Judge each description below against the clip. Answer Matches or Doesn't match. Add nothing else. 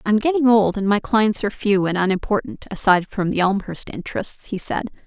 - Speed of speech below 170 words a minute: Doesn't match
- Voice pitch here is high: Matches